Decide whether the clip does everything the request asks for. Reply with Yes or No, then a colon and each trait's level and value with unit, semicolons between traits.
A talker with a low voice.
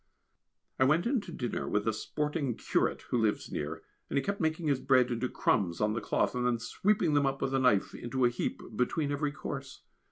Yes: low, 130 Hz